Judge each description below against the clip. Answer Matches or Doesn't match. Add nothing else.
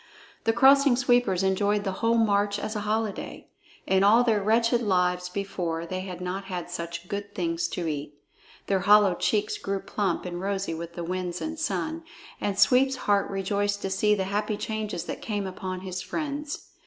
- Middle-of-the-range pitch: Doesn't match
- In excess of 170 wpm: Matches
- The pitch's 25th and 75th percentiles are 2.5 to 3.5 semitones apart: Matches